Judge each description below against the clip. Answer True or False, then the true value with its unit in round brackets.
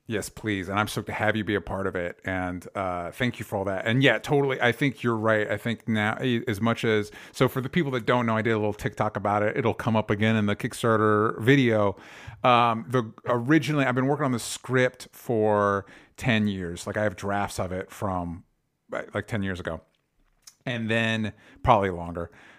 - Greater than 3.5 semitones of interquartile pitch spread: False (3.2 semitones)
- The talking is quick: True (220 wpm)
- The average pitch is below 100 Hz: False (110 Hz)